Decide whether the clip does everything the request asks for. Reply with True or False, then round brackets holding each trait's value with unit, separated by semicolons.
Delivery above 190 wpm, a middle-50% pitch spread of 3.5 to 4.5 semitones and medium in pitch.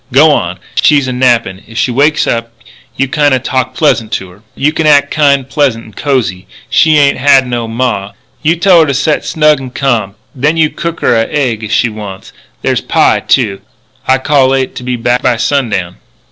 False (200 wpm; 4.1 semitones; 130 Hz)